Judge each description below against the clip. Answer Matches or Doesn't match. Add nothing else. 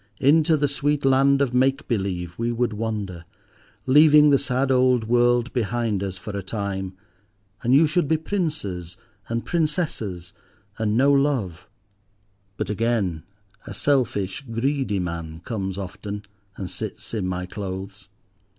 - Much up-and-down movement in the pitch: Matches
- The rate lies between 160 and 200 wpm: Doesn't match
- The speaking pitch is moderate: Doesn't match